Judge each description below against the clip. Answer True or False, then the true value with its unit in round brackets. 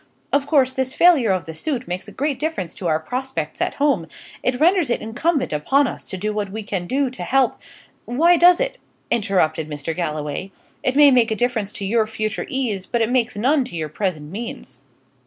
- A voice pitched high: True (235 Hz)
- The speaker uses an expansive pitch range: True (6.3 semitones)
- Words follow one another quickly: True (210 wpm)